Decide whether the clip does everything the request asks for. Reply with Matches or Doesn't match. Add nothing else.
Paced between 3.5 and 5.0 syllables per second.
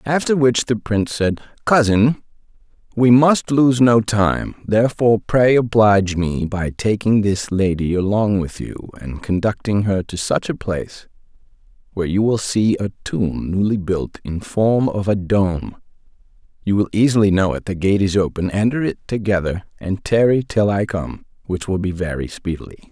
Matches